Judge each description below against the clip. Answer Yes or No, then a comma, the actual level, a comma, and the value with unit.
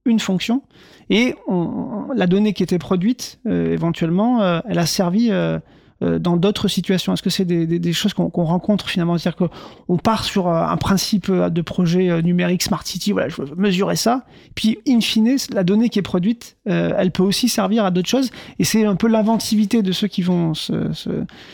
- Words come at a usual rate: Yes, average, 205 wpm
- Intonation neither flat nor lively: Yes, average, 3.7 semitones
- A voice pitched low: No, high, 195 Hz